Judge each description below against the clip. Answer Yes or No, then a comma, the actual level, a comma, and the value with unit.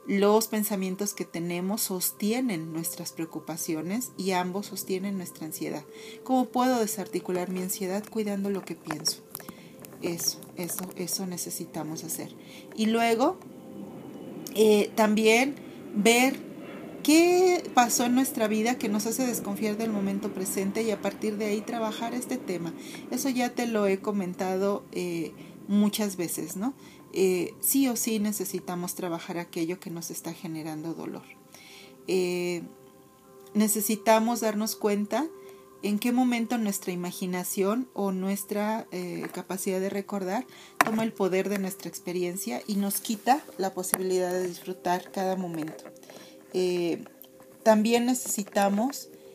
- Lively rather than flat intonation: No, average, 3.7 semitones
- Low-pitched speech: No, high, 200 Hz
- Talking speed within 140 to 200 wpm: No, average, 130 wpm